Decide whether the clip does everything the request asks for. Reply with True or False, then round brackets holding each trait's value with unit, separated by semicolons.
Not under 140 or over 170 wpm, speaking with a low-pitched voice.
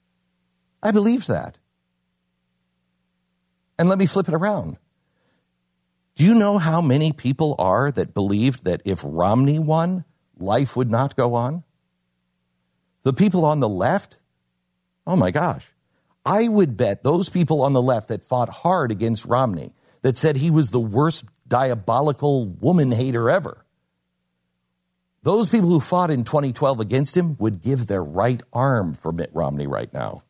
True (150 wpm; 120 Hz)